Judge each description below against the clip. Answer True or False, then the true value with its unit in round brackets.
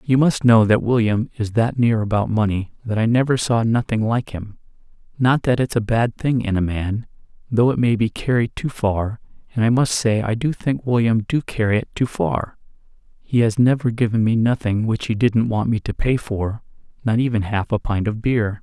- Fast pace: True (215 wpm)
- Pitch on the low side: True (115 Hz)